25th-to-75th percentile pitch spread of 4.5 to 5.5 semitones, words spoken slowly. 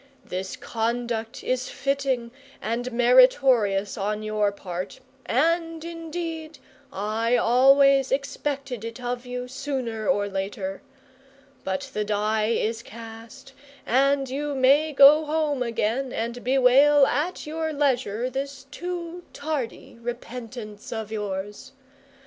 No: average, 4.0 semitones; slow, 115 wpm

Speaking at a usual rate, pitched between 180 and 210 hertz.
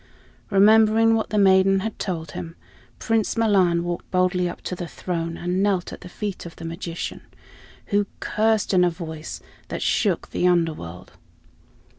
Yes: average, 160 wpm; medium, 185 Hz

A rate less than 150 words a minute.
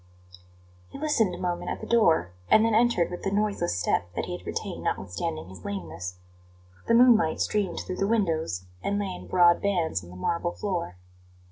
No: average, 190 wpm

